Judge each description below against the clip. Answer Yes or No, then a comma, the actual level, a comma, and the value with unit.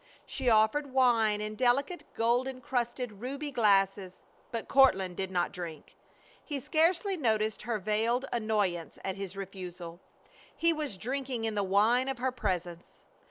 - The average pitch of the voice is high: Yes, high, 225 Hz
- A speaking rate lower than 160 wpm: Yes, average, 145 wpm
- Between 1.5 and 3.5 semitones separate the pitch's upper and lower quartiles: No, average, 5.0 semitones